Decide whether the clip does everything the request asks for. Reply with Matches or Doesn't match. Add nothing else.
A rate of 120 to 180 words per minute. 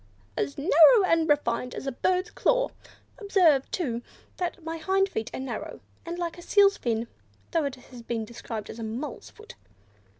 Matches